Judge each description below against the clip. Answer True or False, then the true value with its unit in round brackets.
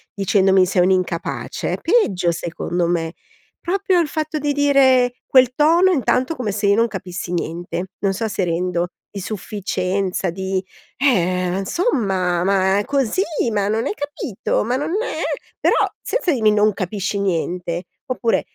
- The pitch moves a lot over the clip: True (6.1 semitones)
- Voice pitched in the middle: False (200 Hz)